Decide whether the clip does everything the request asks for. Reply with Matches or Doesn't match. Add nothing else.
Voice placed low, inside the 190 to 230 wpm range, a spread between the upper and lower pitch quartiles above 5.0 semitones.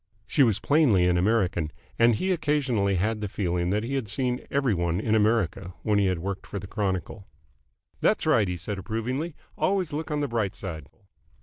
Matches